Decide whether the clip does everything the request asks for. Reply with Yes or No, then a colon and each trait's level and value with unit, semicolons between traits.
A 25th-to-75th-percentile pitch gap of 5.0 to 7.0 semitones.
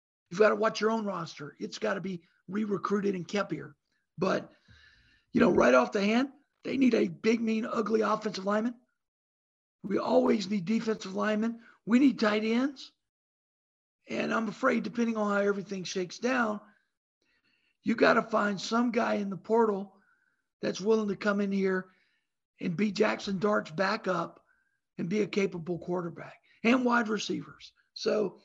No: average, 2.9 semitones